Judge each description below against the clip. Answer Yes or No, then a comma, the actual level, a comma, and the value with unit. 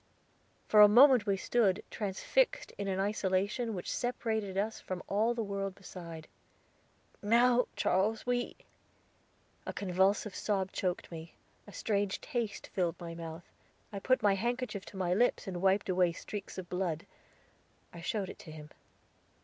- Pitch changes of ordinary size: Yes, average, 3.1 semitones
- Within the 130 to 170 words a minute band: Yes, average, 150 wpm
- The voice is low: No, high, 195 Hz